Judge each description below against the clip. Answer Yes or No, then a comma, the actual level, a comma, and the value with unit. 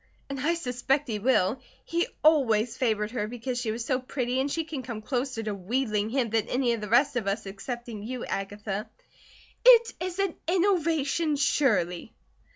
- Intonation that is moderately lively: Yes, average, 4.8 semitones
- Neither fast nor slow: Yes, average, 175 wpm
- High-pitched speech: Yes, very high, 250 Hz